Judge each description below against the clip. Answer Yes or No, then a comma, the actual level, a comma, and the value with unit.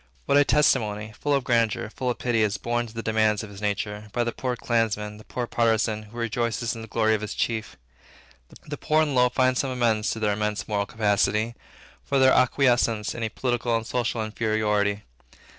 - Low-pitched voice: Yes, low, 115 Hz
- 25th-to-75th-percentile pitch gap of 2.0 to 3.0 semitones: Yes, narrow, 2.4 semitones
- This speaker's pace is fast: Yes, fast, 210 wpm